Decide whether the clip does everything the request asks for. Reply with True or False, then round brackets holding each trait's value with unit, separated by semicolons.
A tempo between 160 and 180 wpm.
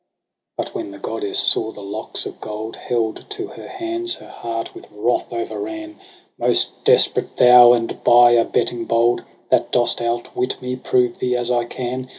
True (170 wpm)